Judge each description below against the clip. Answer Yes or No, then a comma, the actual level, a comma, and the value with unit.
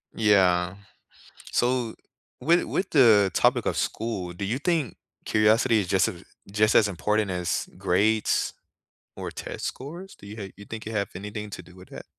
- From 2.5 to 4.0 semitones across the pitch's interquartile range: Yes, average, 3.3 semitones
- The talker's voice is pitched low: Yes, low, 105 Hz